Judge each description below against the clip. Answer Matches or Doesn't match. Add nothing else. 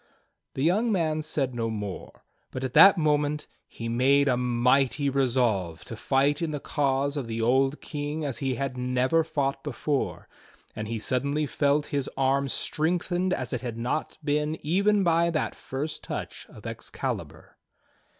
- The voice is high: Doesn't match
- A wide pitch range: Doesn't match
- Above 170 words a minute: Doesn't match